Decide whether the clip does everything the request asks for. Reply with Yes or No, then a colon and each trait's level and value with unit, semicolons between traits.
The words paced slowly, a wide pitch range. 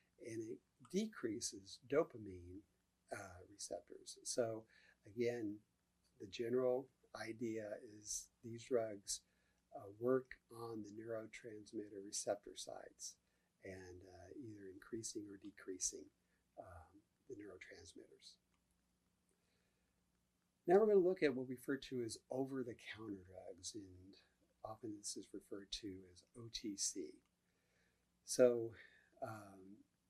Yes: slow, 110 wpm; wide, 7.3 semitones